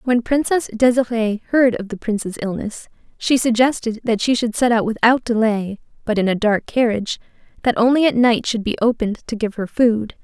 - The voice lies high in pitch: Yes, high, 230 Hz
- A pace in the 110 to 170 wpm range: No, average, 195 wpm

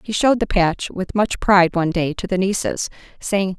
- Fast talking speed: Yes, fast, 220 wpm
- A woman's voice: Yes, female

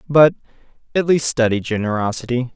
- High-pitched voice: No, low, 130 Hz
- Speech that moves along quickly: No, slow, 120 wpm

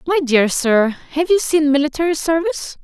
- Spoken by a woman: Yes, female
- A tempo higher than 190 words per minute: No, average, 170 wpm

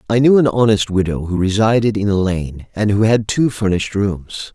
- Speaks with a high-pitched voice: No, low, 105 Hz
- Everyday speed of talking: No, fast, 210 wpm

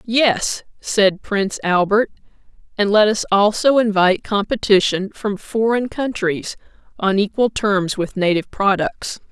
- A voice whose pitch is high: Yes, high, 205 Hz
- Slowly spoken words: Yes, slow, 120 wpm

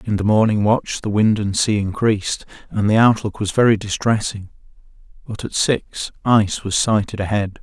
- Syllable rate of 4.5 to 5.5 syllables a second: Yes, 5.0 syllables/s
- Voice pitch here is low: Yes, low, 105 Hz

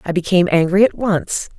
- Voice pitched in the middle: Yes, medium, 180 Hz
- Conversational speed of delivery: Yes, average, 190 wpm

